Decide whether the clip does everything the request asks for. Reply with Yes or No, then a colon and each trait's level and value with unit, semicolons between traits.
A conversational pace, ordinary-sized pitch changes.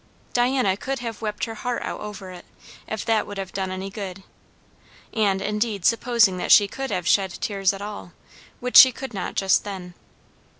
Yes: average, 185 wpm; average, 3.1 semitones